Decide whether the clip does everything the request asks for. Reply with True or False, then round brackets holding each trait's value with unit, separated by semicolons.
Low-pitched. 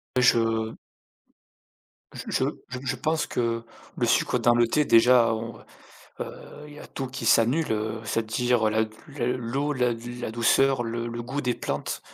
True (120 Hz)